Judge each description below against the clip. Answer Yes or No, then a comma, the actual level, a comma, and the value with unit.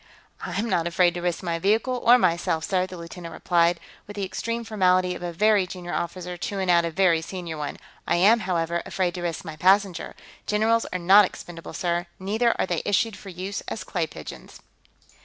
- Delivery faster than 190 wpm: Yes, average, 200 wpm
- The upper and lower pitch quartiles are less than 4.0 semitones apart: Yes, average, 2.8 semitones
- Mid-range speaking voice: Yes, medium, 180 Hz